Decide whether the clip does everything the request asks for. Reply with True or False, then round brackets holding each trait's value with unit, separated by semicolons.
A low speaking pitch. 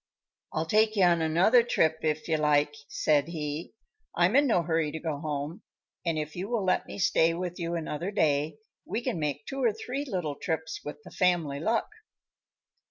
False (165 Hz)